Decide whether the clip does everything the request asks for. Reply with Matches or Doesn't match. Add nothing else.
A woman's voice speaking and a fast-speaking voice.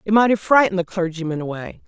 Matches